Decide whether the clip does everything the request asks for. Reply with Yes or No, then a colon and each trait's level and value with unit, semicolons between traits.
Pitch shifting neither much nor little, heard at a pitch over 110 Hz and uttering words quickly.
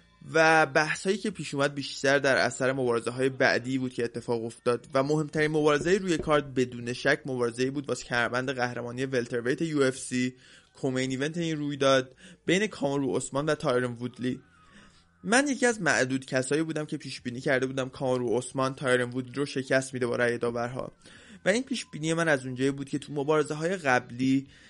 Yes: average, 3.3 semitones; low, 135 Hz; fast, 180 wpm